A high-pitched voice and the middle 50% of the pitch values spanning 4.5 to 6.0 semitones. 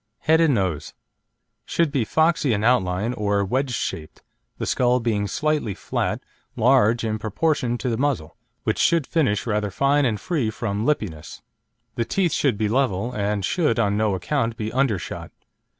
No: low, 115 Hz; average, 5.2 semitones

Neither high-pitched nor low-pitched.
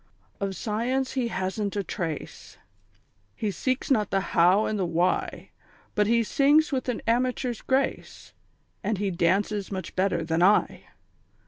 No: high, 210 Hz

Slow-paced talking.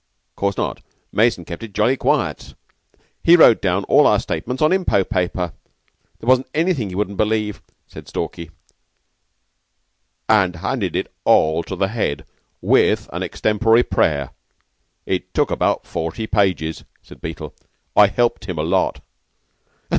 No: average, 145 wpm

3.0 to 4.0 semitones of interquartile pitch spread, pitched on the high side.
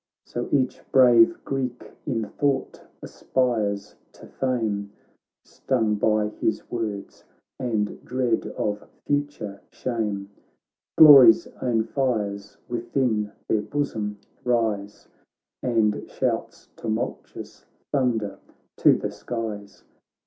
No: average, 3.5 semitones; low, 115 Hz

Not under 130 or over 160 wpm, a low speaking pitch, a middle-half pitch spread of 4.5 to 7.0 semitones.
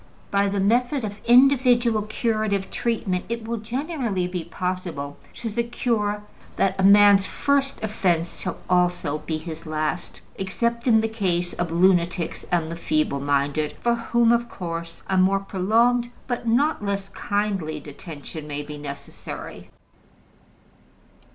No: average, 140 wpm; high, 195 Hz; wide, 5.4 semitones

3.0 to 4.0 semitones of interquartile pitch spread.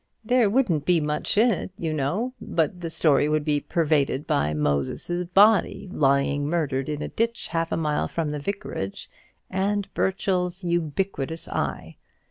No: average, 4.7 semitones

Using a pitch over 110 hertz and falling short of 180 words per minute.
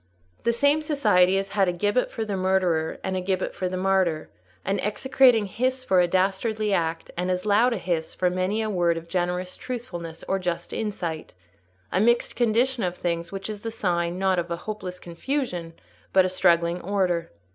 No: high, 190 Hz; average, 190 wpm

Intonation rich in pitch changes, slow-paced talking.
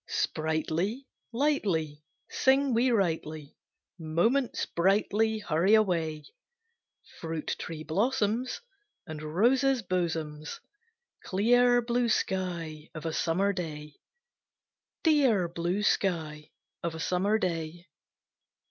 Yes: wide, 6.1 semitones; slow, 95 wpm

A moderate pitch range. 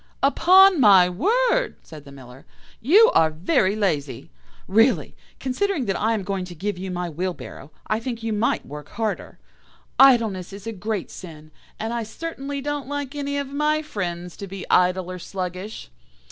No: wide, 7.4 semitones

